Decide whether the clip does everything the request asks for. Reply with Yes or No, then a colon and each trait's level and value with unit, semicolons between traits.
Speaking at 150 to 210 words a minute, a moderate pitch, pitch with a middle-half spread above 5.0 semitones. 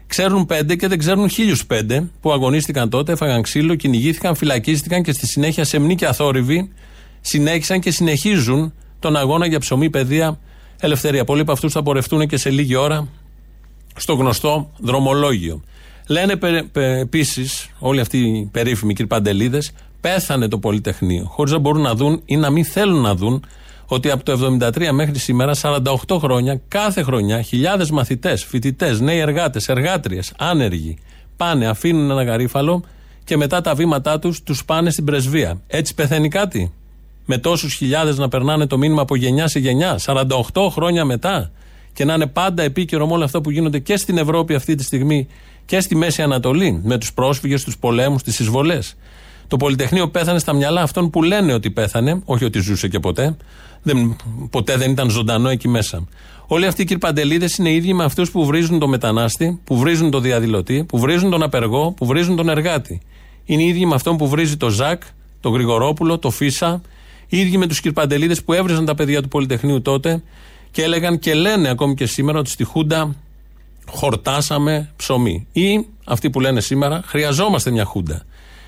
No: fast, 170 wpm; medium, 145 Hz; average, 4.6 semitones